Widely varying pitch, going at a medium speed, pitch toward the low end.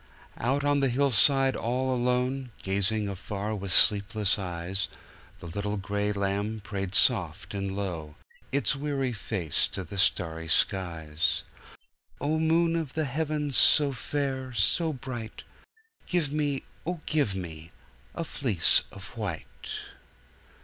No: wide, 6.4 semitones; slow, 120 wpm; low, 110 Hz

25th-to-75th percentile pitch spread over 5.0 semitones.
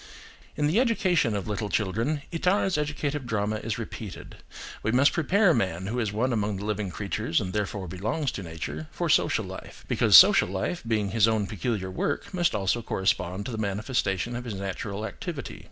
Yes: wide, 5.5 semitones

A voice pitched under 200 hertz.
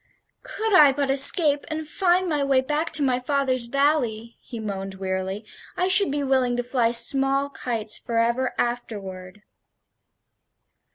No: very high, 260 Hz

